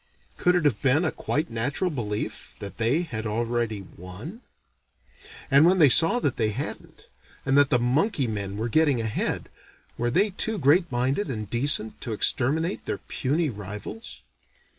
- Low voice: Yes, low, 130 Hz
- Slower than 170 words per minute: Yes, average, 160 wpm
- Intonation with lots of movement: Yes, wide, 6.3 semitones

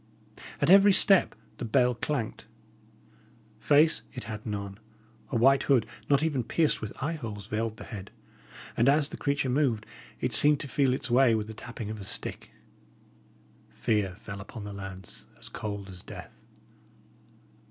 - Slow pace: No, average, 165 wpm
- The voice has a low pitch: Yes, low, 115 Hz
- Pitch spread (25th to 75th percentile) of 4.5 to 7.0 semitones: Yes, average, 5.1 semitones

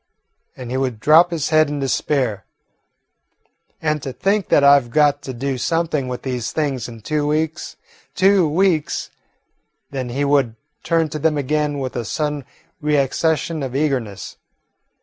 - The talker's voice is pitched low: No, medium, 145 Hz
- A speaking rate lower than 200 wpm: Yes, average, 155 wpm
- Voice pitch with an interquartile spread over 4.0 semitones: No, average, 3.0 semitones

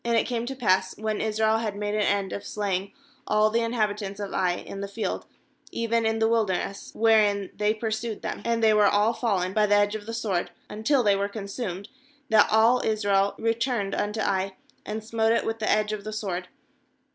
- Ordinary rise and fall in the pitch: No, narrow, 1.9 semitones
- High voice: Yes, high, 215 Hz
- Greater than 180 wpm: Yes, fast, 205 wpm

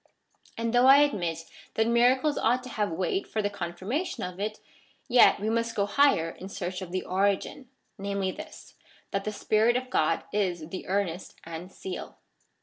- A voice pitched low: No, high, 200 Hz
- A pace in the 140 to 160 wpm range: No, average, 175 wpm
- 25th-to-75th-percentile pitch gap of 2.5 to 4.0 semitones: No, average, 4.6 semitones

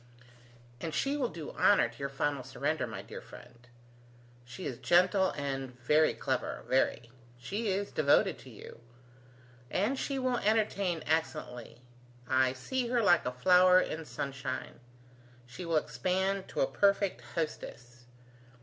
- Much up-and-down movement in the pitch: Yes, wide, 7.2 semitones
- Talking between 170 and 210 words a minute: No, average, 140 wpm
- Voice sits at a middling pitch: Yes, medium, 155 Hz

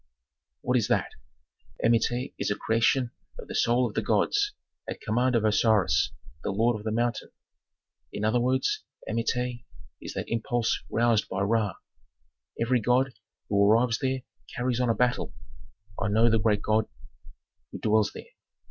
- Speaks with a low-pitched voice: Yes, low, 115 Hz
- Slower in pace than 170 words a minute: Yes, average, 155 wpm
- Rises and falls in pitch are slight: Yes, narrow, 2.3 semitones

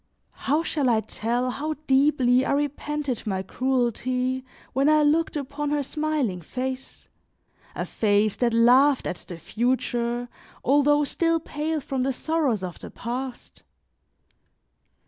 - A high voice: Yes, very high, 260 Hz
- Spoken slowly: Yes, slow, 130 wpm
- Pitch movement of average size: Yes, average, 3.5 semitones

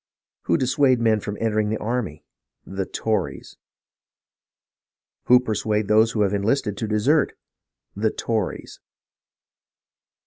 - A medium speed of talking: No, slow, 110 wpm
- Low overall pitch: Yes, low, 110 Hz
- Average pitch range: No, narrow, 2.3 semitones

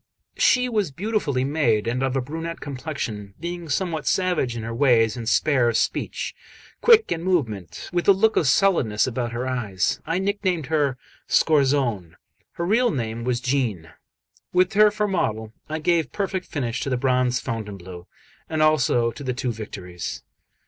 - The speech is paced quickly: No, average, 165 wpm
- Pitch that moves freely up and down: Yes, wide, 6.7 semitones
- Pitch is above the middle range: No, low, 135 Hz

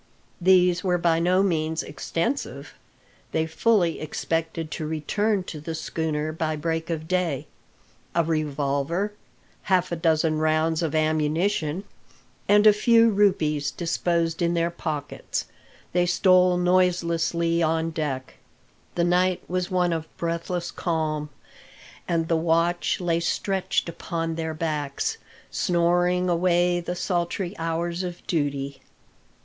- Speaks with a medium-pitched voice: Yes, medium, 170 Hz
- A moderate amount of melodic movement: No, narrow, 2.1 semitones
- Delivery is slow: Yes, slow, 125 wpm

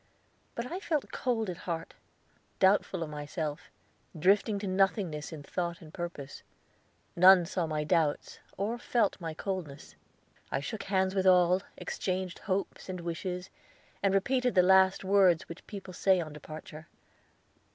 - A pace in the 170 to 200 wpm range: No, average, 145 wpm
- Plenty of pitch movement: No, average, 3.1 semitones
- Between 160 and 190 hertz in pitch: Yes, medium, 185 Hz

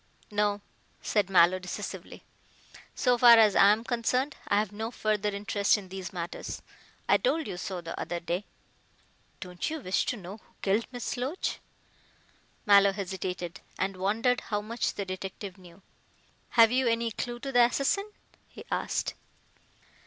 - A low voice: No, high, 205 Hz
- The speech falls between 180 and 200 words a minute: No, average, 155 wpm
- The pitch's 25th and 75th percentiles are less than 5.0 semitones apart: Yes, average, 3.9 semitones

